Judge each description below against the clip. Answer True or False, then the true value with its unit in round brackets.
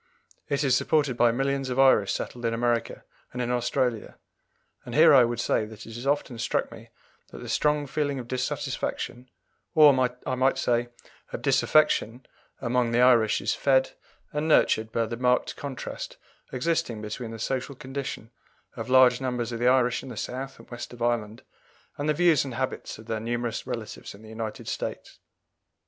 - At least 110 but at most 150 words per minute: False (180 wpm)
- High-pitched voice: False (125 Hz)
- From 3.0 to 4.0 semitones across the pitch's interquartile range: False (2.4 semitones)